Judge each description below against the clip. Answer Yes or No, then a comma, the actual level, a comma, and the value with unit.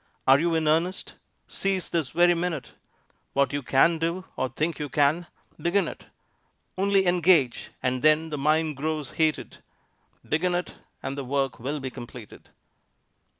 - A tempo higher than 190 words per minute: No, average, 150 wpm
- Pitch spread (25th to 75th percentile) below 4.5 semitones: Yes, average, 3.8 semitones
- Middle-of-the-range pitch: Yes, medium, 155 Hz